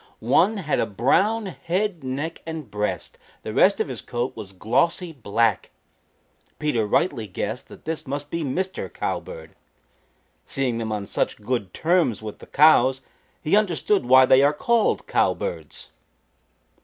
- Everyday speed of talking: Yes, average, 145 wpm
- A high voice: No, low, 135 Hz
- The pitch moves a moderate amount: No, wide, 6.7 semitones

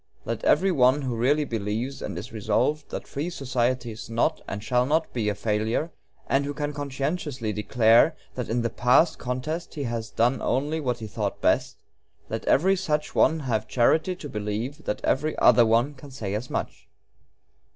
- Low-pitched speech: Yes, low, 125 Hz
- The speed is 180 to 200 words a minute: Yes, average, 185 wpm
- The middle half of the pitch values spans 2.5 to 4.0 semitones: No, average, 4.6 semitones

